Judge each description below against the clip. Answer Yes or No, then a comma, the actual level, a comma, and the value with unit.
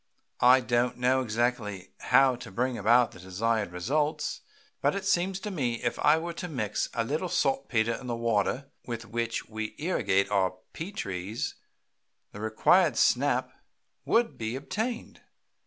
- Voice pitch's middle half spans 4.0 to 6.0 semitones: Yes, average, 4.7 semitones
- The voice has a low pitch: Yes, low, 120 Hz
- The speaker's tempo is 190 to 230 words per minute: No, average, 155 wpm